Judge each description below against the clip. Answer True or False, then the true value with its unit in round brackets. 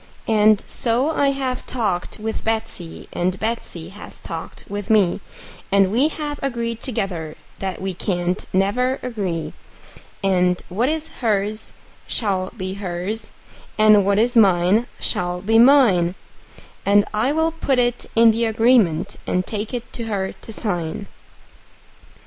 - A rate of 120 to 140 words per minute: True (135 wpm)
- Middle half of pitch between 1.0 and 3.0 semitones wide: False (4.2 semitones)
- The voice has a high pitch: True (210 Hz)